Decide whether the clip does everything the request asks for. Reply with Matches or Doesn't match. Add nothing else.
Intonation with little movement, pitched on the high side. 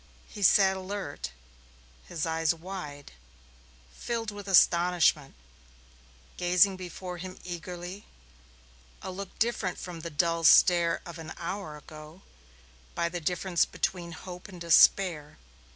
Doesn't match